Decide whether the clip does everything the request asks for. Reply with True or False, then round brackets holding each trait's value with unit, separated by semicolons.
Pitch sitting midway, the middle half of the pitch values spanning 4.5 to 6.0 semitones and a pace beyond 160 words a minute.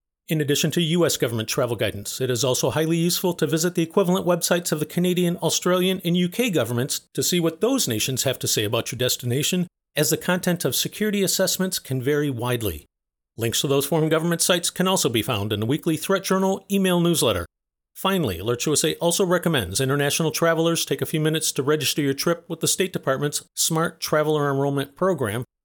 True (160 Hz; 4.9 semitones; 195 wpm)